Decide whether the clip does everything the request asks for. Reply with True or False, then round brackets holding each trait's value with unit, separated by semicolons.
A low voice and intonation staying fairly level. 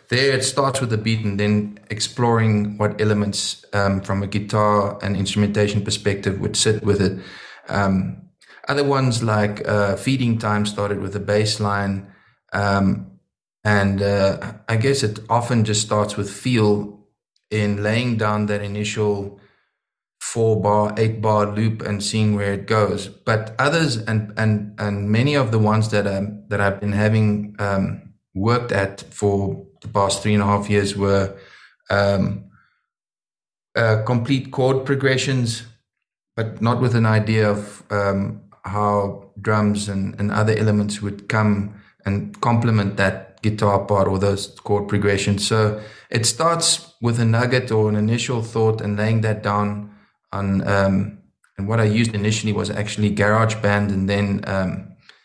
True (105 Hz; 1.6 semitones)